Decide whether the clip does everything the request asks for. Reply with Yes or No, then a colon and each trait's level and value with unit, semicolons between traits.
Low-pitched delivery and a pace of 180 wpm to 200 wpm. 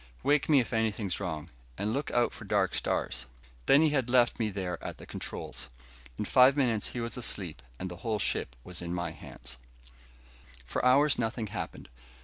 Yes: low, 110 Hz; average, 185 wpm